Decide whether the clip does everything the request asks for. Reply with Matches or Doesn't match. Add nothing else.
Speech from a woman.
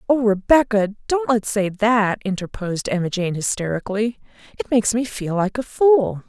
Matches